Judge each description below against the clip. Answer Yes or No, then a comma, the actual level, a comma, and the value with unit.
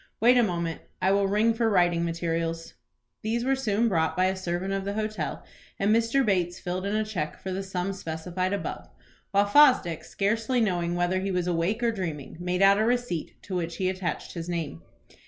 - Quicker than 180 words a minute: Yes, average, 200 wpm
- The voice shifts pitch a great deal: No, average, 3.7 semitones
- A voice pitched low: No, high, 190 Hz